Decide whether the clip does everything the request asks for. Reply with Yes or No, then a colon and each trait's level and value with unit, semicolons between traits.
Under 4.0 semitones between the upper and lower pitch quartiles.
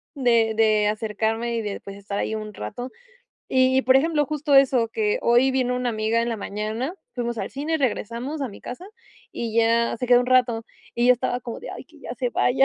Yes: average, 2.8 semitones